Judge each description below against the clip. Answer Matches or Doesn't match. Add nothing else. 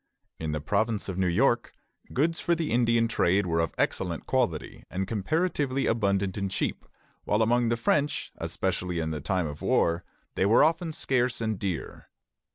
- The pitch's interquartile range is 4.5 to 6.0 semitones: Matches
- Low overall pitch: Matches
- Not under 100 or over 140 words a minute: Doesn't match